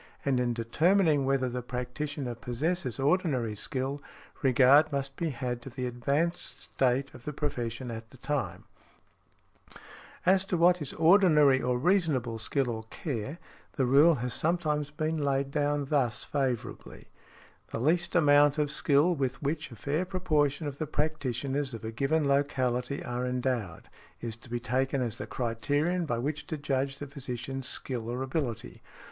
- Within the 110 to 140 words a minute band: No, average, 160 wpm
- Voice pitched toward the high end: No, medium, 140 Hz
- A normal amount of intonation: Yes, average, 3.4 semitones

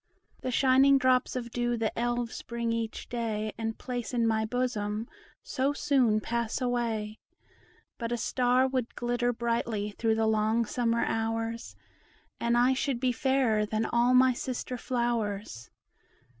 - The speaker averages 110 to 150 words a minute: Yes, average, 145 wpm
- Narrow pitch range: Yes, narrow, 2.0 semitones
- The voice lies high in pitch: Yes, high, 235 Hz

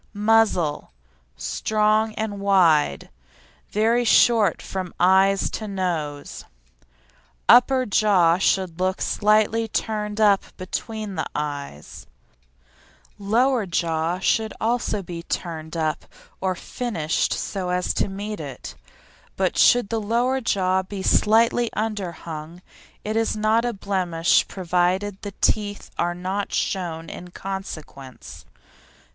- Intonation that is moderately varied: Yes, average, 3.7 semitones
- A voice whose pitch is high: Yes, high, 195 Hz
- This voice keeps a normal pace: No, slow, 115 wpm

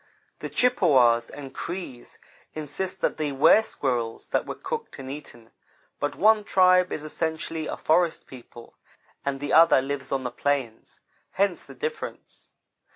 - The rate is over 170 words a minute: No, average, 150 wpm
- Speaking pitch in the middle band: Yes, medium, 150 Hz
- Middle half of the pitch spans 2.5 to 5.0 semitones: No, wide, 5.6 semitones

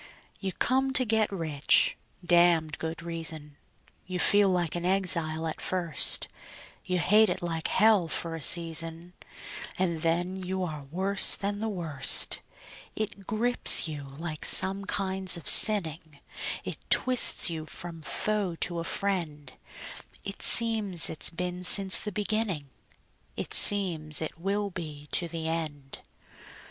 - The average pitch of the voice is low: No, medium, 175 Hz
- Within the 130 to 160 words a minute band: Yes, average, 140 wpm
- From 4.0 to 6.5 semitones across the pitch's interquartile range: No, average, 3.5 semitones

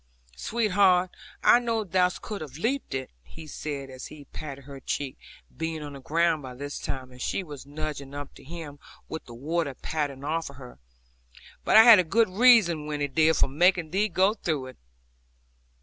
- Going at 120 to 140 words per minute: No, average, 180 wpm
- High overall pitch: No, medium, 155 Hz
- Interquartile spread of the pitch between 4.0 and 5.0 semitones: Yes, average, 4.6 semitones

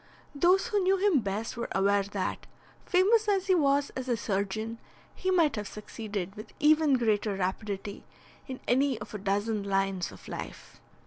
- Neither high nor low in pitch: No, high, 225 Hz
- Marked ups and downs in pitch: Yes, wide, 7.3 semitones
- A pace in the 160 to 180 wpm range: Yes, average, 170 wpm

